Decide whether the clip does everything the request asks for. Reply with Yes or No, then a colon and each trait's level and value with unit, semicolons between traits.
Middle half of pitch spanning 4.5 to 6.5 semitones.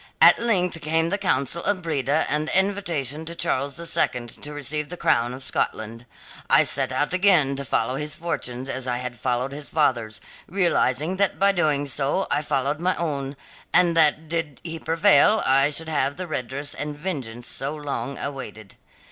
No: average, 4.1 semitones